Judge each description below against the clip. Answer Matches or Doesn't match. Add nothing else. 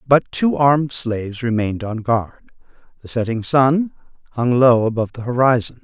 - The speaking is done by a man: Matches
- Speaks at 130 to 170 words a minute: Matches